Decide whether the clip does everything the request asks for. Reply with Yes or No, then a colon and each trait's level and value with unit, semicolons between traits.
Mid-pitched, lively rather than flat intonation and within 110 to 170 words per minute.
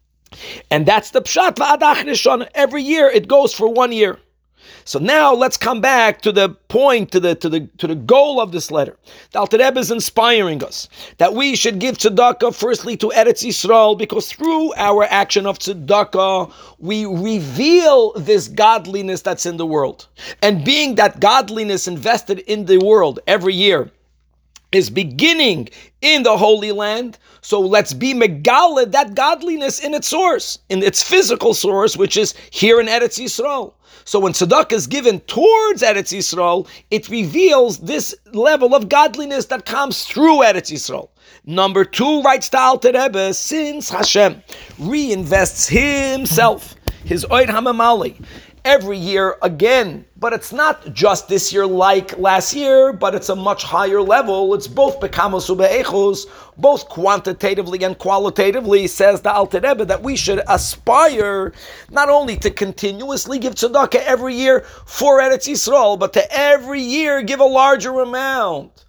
No: high, 225 Hz; wide, 5.8 semitones; average, 150 wpm